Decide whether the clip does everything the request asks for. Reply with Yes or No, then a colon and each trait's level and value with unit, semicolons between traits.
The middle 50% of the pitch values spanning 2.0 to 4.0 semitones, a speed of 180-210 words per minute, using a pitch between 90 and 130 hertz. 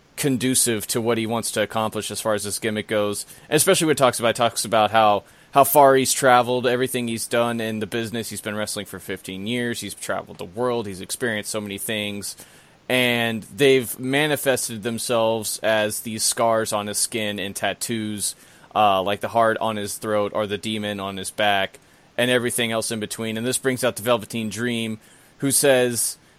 Yes: average, 2.9 semitones; average, 200 wpm; low, 110 Hz